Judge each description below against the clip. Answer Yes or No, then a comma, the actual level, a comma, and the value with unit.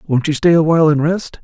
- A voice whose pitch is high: No, medium, 155 Hz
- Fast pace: Yes, fast, 250 wpm